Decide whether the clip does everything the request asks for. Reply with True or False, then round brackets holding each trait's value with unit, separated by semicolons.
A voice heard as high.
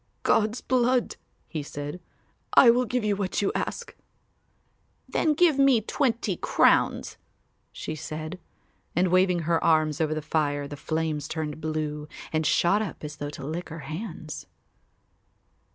False (165 Hz)